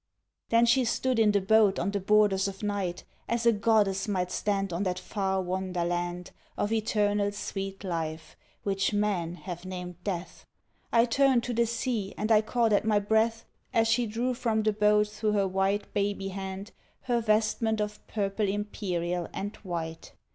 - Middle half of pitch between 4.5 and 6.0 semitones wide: No, narrow, 2.5 semitones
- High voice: Yes, high, 205 Hz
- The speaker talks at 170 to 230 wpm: Yes, average, 175 wpm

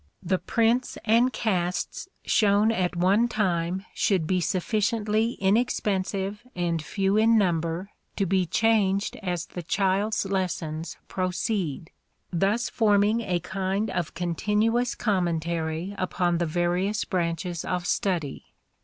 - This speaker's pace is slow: Yes, slow, 120 wpm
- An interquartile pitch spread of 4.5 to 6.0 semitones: No, average, 3.4 semitones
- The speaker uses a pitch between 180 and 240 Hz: Yes, high, 190 Hz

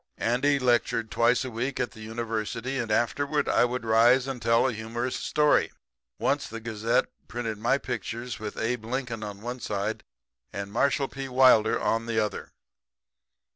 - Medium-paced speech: Yes, average, 165 wpm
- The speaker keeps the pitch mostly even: Yes, narrow, 2.3 semitones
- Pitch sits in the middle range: No, low, 120 Hz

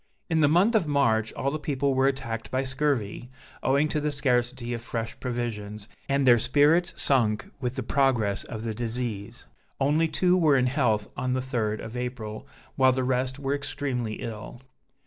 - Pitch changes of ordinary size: Yes, average, 3.5 semitones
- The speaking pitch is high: No, low, 130 Hz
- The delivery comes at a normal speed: Yes, average, 180 wpm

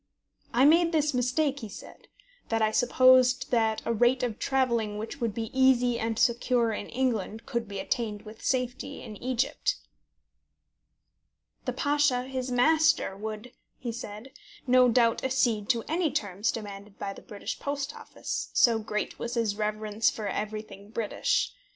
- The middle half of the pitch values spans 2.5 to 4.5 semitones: Yes, average, 3.3 semitones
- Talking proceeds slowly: No, average, 155 wpm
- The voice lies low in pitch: No, high, 235 Hz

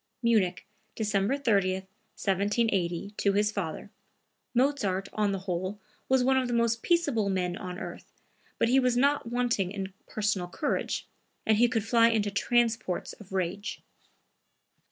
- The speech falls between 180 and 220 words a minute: No, average, 145 wpm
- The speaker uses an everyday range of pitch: Yes, average, 3.6 semitones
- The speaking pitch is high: Yes, high, 210 Hz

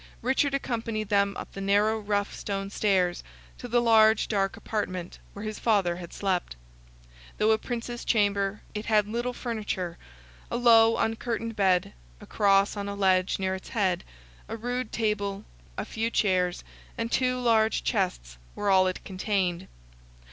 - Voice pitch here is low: No, high, 205 Hz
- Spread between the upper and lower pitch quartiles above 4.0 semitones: No, average, 2.8 semitones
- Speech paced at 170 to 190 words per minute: No, average, 155 wpm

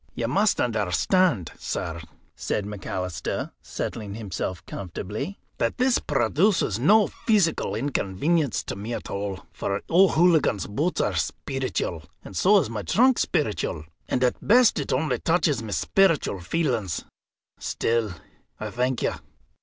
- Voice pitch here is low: Yes, low, 125 Hz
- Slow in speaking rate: Yes, slow, 130 wpm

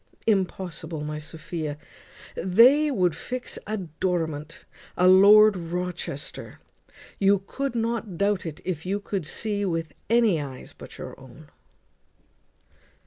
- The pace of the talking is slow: Yes, slow, 125 wpm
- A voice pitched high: No, medium, 180 Hz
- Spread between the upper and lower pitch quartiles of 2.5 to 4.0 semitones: No, average, 4.5 semitones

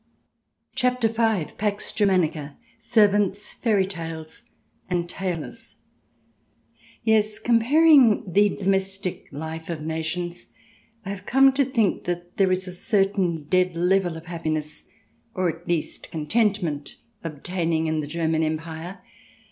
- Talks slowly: Yes, slow, 120 wpm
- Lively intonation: No, average, 4.2 semitones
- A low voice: No, medium, 180 Hz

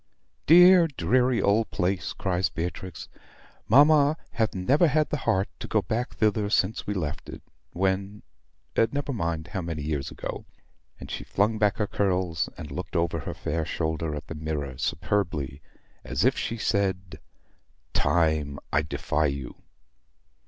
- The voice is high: No, very low, 95 Hz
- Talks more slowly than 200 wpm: Yes, average, 150 wpm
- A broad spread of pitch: Yes, wide, 5.7 semitones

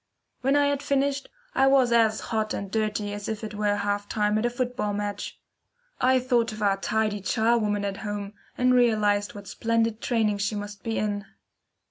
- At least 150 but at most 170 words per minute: No, average, 185 wpm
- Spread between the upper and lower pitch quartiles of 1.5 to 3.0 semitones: Yes, narrow, 2.6 semitones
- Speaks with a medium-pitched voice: No, high, 215 Hz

